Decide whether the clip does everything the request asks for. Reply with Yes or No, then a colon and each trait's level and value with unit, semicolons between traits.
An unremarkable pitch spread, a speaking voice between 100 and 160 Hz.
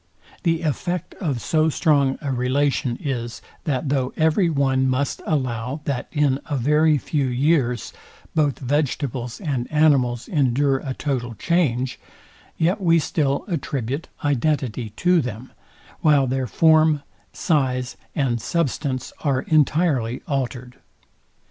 Yes: average, 3.5 semitones; medium, 140 Hz